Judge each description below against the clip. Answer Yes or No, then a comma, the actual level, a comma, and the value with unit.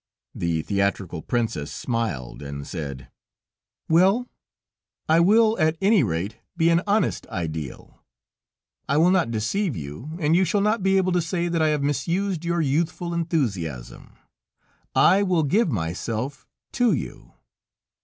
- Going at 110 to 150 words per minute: Yes, average, 140 wpm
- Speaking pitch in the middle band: Yes, medium, 155 Hz